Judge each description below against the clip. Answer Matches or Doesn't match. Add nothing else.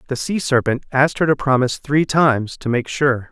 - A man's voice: Matches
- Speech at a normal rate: Doesn't match